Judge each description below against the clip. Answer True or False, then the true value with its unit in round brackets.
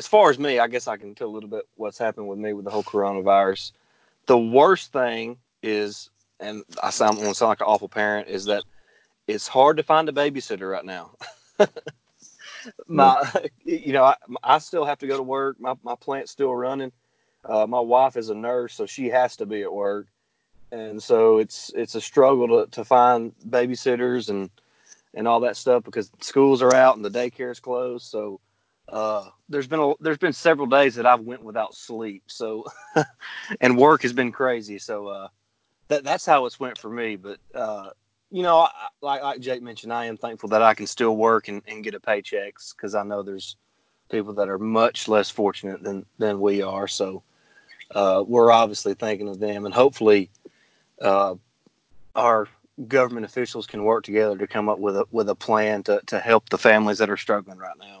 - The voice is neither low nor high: False (115 Hz)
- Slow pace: False (200 wpm)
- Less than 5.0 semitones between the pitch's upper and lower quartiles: True (3.3 semitones)